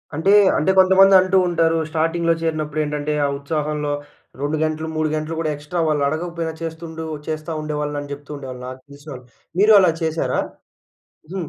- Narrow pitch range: Yes, narrow, 2.0 semitones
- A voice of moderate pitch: Yes, medium, 155 Hz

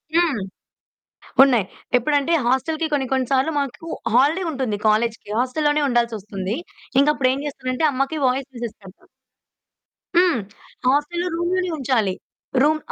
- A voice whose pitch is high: Yes, very high, 265 Hz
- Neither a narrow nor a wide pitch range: Yes, average, 4.3 semitones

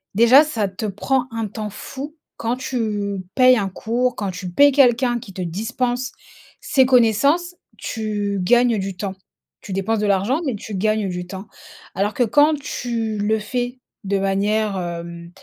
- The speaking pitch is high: Yes, high, 220 Hz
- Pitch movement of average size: Yes, average, 4.1 semitones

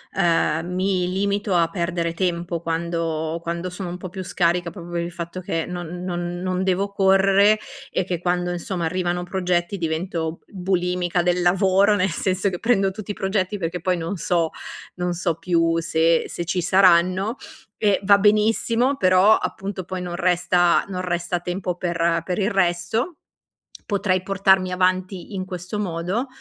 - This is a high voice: No, medium, 180 Hz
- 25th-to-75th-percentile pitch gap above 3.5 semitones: No, narrow, 1.8 semitones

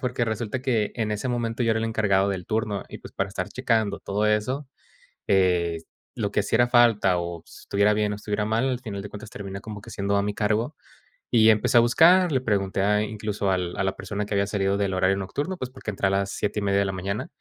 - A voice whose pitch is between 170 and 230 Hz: No, low, 105 Hz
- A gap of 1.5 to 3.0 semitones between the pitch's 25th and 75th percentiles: Yes, narrow, 2.6 semitones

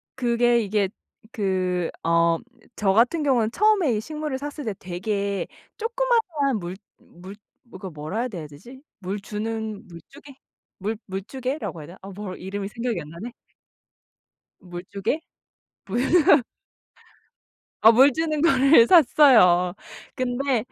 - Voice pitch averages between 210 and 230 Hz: Yes, high, 220 Hz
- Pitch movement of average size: No, wide, 6.3 semitones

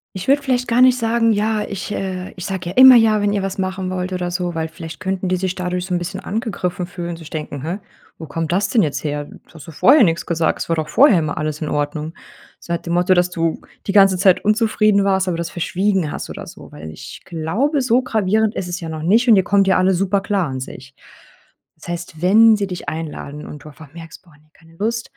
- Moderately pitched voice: Yes, medium, 180 Hz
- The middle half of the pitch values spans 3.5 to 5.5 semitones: Yes, average, 3.9 semitones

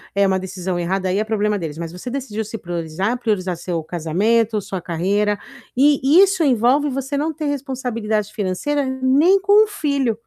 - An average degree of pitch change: No, wide, 6.6 semitones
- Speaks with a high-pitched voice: Yes, high, 220 Hz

